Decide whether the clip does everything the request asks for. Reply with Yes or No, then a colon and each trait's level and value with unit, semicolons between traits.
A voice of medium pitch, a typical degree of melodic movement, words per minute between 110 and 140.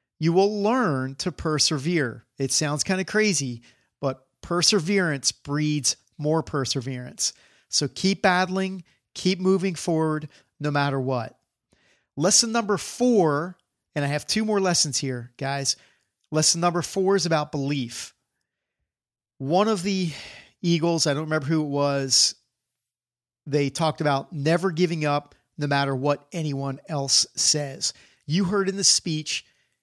Yes: medium, 155 Hz; average, 4.8 semitones; slow, 135 wpm